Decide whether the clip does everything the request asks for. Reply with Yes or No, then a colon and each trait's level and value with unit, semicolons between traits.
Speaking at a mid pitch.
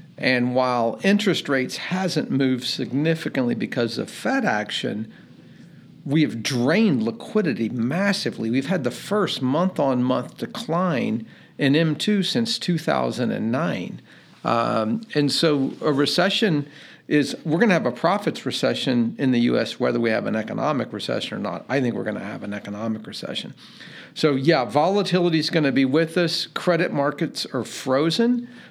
Yes: medium, 150 Hz